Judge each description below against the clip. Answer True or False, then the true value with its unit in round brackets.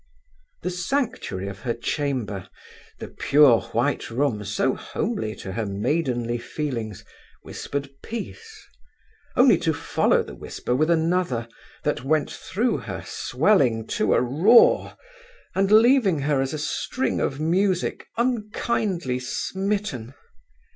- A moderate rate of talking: False (120 wpm)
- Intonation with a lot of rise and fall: True (8.7 semitones)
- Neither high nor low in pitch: True (150 Hz)